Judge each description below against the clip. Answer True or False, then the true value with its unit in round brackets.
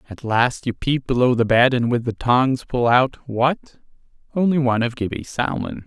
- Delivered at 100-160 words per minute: False (175 wpm)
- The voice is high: False (125 Hz)